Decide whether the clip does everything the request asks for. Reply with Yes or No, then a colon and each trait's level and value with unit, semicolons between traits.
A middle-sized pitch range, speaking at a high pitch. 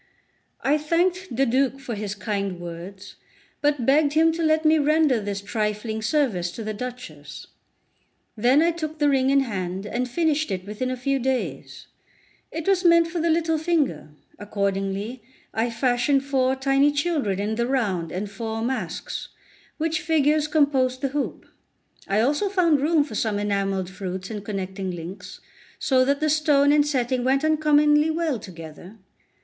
No: wide, 6.6 semitones; very high, 260 Hz